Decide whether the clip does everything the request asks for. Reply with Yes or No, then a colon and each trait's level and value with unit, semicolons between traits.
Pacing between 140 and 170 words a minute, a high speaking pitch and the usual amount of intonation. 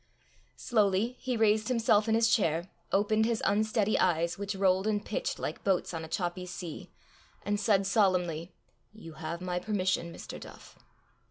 Yes: average, 160 wpm; high, 195 Hz; average, 3.4 semitones